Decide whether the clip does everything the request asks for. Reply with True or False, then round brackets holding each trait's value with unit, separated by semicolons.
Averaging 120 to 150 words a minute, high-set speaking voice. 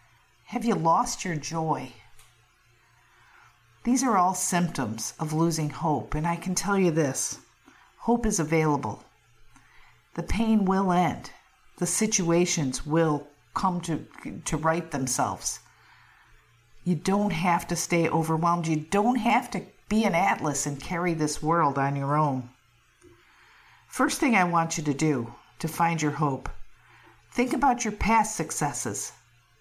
False (140 wpm; 165 Hz)